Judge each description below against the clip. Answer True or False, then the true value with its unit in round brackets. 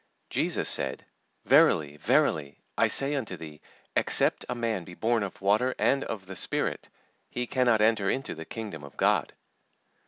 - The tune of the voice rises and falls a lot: True (6.7 semitones)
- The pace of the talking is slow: False (160 wpm)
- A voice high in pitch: False (105 Hz)